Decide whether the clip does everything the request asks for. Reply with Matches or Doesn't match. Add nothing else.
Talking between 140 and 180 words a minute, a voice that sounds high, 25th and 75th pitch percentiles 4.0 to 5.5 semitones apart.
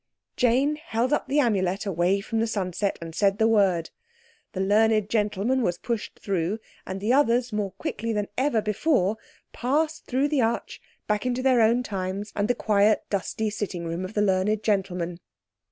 Doesn't match